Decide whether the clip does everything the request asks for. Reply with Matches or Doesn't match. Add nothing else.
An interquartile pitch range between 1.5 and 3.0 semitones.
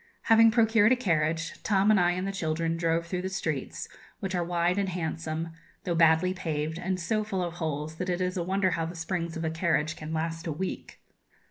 Matches